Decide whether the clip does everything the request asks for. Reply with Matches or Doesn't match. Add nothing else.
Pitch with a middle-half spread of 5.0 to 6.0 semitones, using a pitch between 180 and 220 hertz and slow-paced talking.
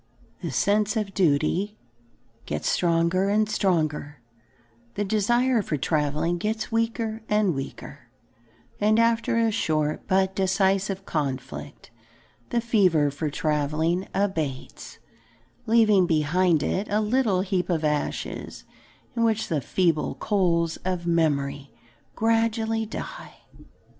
Matches